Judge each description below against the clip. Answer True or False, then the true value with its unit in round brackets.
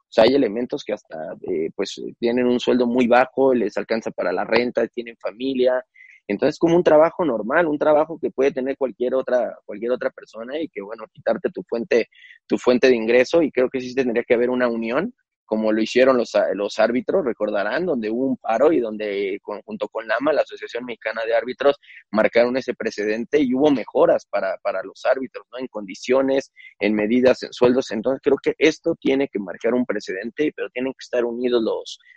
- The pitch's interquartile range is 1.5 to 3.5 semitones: False (3.9 semitones)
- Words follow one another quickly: True (200 wpm)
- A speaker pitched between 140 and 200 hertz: False (130 Hz)